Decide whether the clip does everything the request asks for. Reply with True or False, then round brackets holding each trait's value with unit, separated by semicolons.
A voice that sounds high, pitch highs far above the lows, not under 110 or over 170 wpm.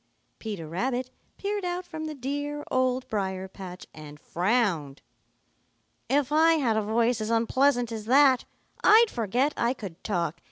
True (240 Hz; 6.5 semitones; 150 wpm)